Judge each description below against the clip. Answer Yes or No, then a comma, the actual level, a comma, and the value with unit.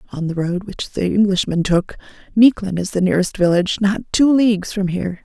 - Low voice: No, high, 195 Hz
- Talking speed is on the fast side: No, average, 195 wpm